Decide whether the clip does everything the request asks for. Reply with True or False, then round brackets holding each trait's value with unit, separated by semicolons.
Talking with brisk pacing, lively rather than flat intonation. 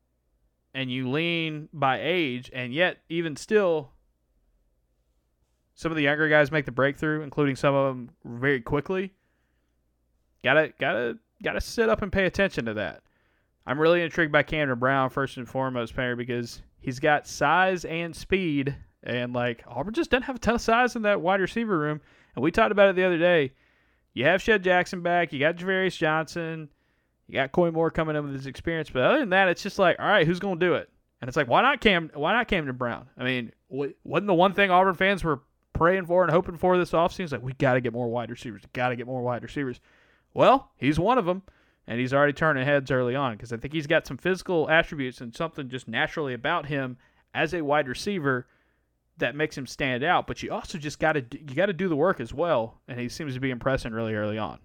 True (225 wpm; 5.7 semitones)